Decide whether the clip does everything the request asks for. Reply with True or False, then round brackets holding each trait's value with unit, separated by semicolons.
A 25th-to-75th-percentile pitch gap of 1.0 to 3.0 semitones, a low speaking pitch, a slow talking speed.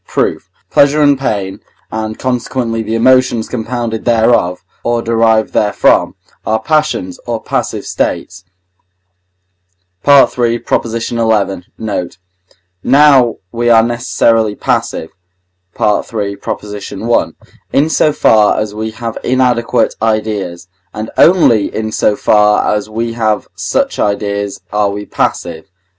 True (2.4 semitones; 110 Hz; 115 wpm)